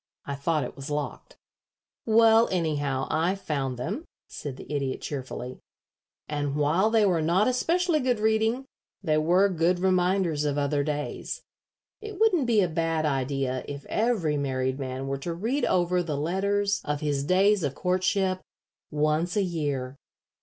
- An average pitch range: No, wide, 5.7 semitones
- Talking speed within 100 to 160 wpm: Yes, average, 155 wpm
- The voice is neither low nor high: Yes, medium, 165 Hz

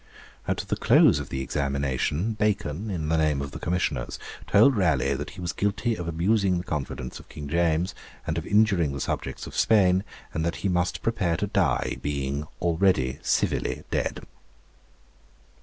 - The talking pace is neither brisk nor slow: Yes, average, 170 wpm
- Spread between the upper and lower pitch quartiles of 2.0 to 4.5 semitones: No, average, 5.2 semitones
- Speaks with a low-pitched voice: Yes, very low, 85 Hz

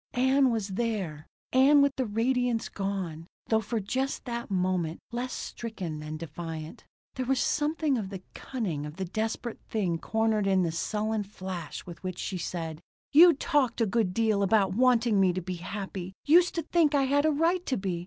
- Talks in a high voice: Yes, high, 215 Hz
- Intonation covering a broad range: Yes, wide, 5.8 semitones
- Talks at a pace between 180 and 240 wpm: Yes, average, 185 wpm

